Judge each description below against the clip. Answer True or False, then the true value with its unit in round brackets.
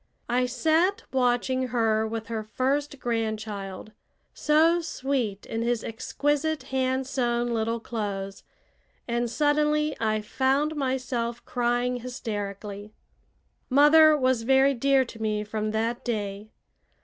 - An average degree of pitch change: True (3.7 semitones)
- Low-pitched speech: False (240 Hz)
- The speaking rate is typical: False (115 wpm)